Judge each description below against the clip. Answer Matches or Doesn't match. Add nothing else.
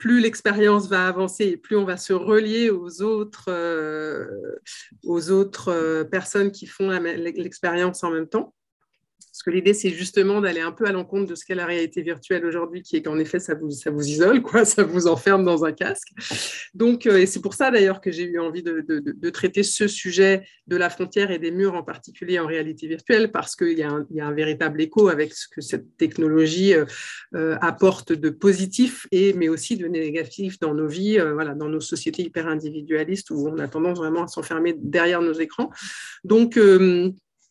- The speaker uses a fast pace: Doesn't match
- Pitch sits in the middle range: Matches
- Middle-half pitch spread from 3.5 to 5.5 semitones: Matches